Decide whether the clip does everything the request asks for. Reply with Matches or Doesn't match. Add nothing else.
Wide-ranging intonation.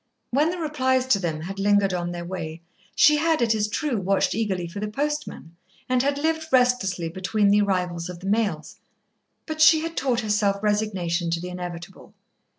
Matches